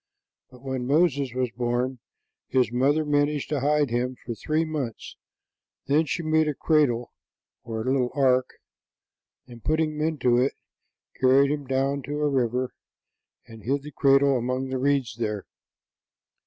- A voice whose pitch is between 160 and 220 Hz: No, low, 135 Hz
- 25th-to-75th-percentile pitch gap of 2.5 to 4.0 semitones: Yes, average, 2.9 semitones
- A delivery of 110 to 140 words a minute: No, average, 150 wpm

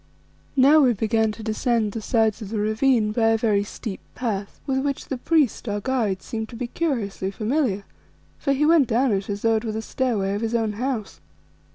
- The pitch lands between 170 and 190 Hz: No, high, 225 Hz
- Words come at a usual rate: No, fast, 210 wpm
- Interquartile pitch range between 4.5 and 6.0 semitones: No, average, 3.7 semitones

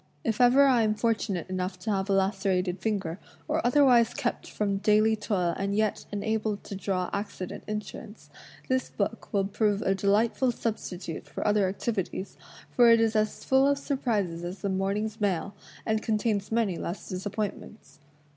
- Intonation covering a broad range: No, narrow, 2.5 semitones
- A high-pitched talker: Yes, high, 210 Hz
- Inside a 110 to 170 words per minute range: Yes, average, 165 wpm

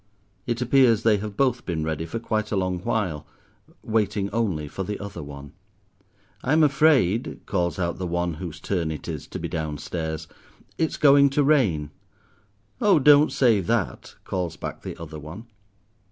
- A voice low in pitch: Yes, low, 100 Hz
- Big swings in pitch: Yes, wide, 6.7 semitones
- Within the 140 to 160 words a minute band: No, average, 170 wpm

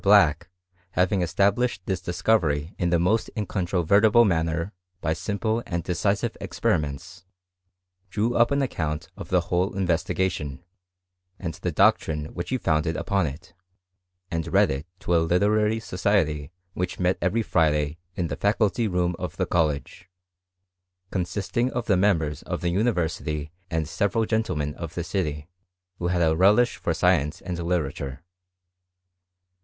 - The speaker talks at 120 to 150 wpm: Yes, average, 145 wpm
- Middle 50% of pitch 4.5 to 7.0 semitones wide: No, average, 4.1 semitones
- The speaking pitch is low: Yes, very low, 90 Hz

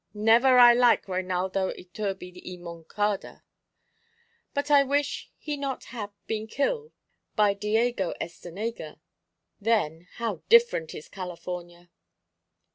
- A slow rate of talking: Yes, slow, 110 wpm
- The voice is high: Yes, high, 205 Hz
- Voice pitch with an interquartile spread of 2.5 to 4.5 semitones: No, average, 5.3 semitones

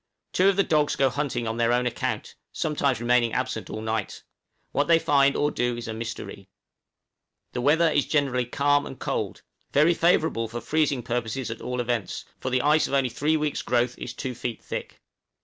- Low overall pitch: Yes, low, 130 Hz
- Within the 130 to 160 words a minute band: No, average, 195 wpm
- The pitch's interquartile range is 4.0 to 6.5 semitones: No, average, 3.6 semitones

